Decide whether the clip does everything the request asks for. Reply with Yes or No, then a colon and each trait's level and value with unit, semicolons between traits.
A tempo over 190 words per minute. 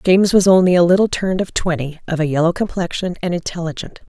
Yes: average, 200 wpm